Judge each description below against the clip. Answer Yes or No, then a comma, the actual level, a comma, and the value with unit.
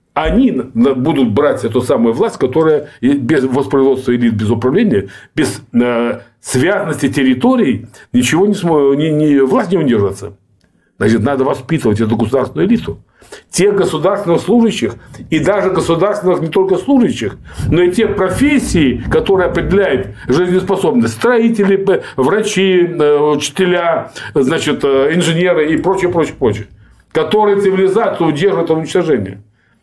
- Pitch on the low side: No, medium, 160 Hz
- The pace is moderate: Yes, average, 120 wpm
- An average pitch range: No, wide, 6.8 semitones